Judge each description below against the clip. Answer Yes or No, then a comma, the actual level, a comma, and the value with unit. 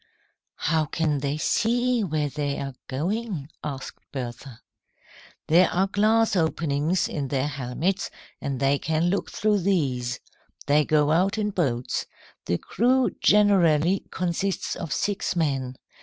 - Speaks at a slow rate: Yes, slow, 130 wpm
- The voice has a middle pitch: Yes, medium, 160 Hz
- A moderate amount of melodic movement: No, wide, 5.7 semitones